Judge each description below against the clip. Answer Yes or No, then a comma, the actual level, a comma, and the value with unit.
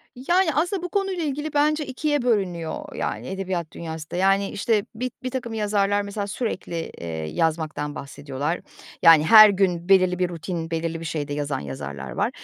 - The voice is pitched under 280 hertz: Yes, high, 190 Hz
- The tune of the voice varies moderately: No, wide, 7.1 semitones